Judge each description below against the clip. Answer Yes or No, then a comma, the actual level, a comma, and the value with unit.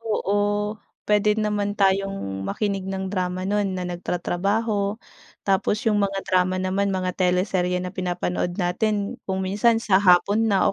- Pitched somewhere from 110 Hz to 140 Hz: No, high, 195 Hz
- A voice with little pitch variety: Yes, narrow, 2.1 semitones